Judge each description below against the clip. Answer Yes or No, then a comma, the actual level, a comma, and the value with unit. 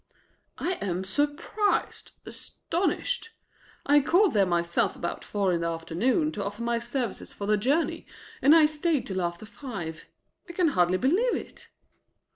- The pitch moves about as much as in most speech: No, wide, 8.8 semitones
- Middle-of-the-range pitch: No, high, 235 Hz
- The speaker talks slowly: No, average, 155 wpm